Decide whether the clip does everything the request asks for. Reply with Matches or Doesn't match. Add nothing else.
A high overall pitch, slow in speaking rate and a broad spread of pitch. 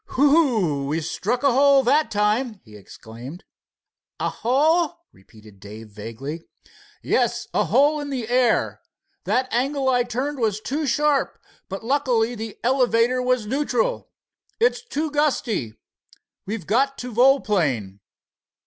Matches